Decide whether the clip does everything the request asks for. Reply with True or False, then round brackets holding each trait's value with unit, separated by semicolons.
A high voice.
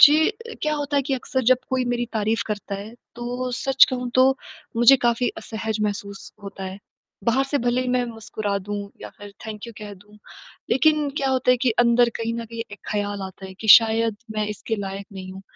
True (225 Hz)